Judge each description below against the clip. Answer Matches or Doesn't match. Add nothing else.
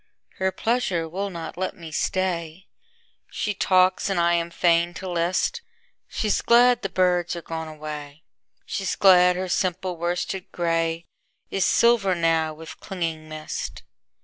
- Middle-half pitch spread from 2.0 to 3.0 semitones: Matches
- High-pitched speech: Doesn't match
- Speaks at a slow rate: Matches